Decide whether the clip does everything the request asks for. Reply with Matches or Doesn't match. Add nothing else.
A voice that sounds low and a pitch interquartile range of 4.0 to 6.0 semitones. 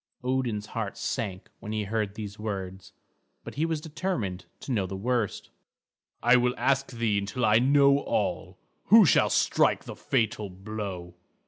Matches